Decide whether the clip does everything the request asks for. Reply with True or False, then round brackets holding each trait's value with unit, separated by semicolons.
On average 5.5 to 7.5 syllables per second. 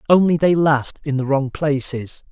False (4.9 syllables/s)